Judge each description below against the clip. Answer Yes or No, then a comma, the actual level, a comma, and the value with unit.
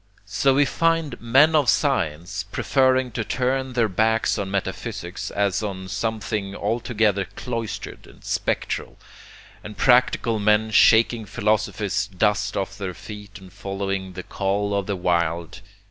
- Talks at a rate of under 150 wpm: Yes, slow, 135 wpm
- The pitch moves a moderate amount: Yes, average, 3.3 semitones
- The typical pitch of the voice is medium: No, low, 105 Hz